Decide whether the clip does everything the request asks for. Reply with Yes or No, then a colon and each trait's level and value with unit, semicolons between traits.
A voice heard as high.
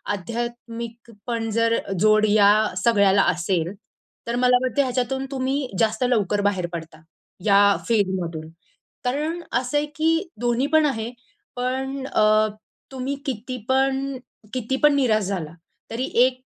Yes: high, 235 Hz